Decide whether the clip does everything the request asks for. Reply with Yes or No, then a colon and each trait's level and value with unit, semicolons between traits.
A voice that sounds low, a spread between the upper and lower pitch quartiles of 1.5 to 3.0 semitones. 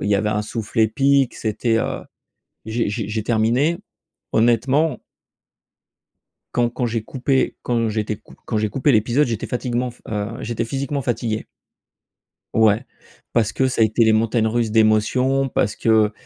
Yes: low, 115 Hz; narrow, 2.6 semitones